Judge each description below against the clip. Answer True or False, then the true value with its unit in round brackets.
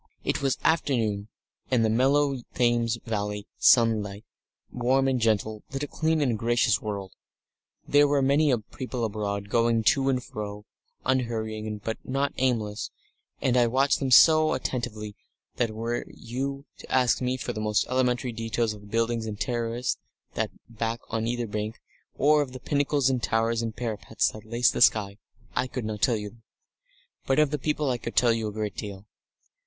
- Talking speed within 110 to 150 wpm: False (175 wpm)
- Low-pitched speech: True (115 Hz)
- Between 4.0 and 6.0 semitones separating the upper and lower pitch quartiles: False (3.2 semitones)